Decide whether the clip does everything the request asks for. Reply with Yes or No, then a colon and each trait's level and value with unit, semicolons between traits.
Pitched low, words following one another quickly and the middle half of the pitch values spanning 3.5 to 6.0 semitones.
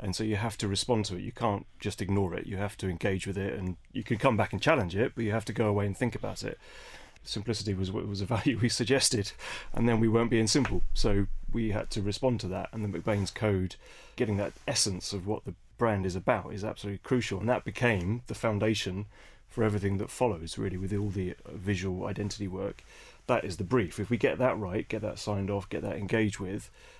No: low, 105 Hz; fast, 235 wpm; narrow, 2.6 semitones